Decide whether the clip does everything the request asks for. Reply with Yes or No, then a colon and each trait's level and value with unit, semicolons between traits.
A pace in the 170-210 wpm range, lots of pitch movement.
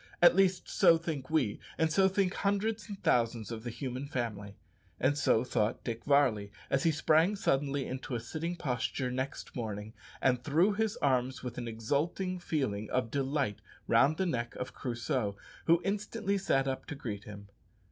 Yes: average, 175 wpm; wide, 6.1 semitones